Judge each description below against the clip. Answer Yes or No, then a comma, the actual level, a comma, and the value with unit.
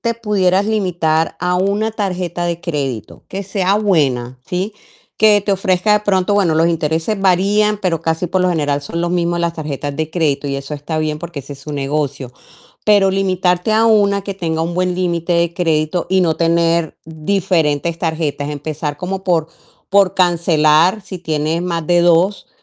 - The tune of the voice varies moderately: Yes, average, 3.5 semitones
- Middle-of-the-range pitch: Yes, medium, 170 Hz